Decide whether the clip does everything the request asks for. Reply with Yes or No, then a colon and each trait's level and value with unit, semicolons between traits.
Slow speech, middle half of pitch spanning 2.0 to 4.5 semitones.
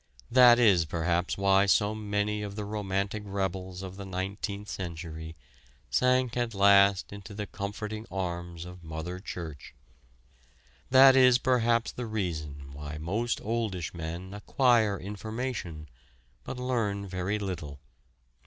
Yes: slow, 125 wpm; average, 3.6 semitones